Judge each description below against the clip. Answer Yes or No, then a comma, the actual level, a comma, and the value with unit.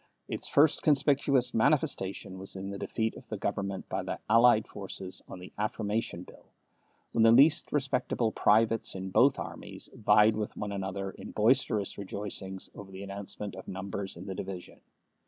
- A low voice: Yes, low, 105 Hz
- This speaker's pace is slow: No, average, 165 wpm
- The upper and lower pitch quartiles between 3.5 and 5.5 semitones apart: No, average, 3.1 semitones